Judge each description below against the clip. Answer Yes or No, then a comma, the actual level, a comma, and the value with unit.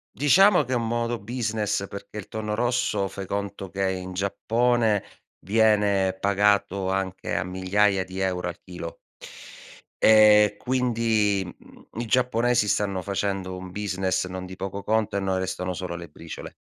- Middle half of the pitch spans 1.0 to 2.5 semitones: No, average, 2.9 semitones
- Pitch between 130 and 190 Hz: No, low, 100 Hz